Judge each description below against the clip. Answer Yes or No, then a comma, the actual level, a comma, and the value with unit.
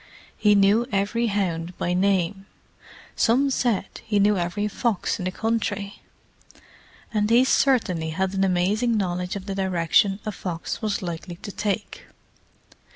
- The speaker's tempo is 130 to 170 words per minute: Yes, average, 145 wpm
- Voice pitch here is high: Yes, high, 200 Hz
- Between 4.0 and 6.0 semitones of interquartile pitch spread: No, average, 2.9 semitones